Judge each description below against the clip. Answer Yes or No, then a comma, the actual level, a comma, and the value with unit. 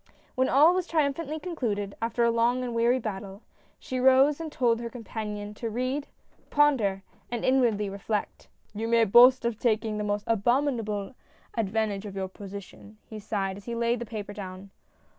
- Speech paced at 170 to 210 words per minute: Yes, average, 180 wpm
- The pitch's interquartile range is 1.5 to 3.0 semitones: No, average, 3.7 semitones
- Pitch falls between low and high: No, high, 230 Hz